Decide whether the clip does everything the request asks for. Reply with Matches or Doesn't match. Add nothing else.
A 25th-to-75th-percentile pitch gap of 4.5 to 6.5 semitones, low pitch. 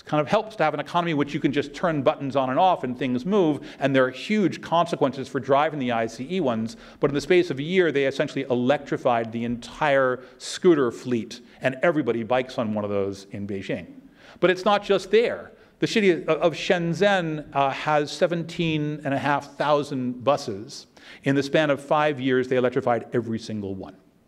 Doesn't match